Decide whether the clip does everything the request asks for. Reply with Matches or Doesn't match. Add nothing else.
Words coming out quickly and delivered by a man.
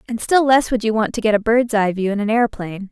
Doesn't match